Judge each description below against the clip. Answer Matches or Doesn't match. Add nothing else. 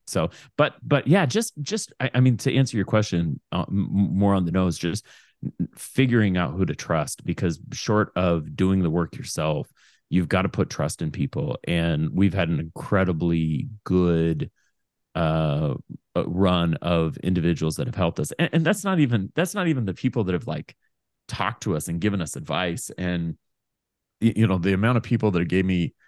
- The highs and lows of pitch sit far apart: Matches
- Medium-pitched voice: Doesn't match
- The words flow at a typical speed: Matches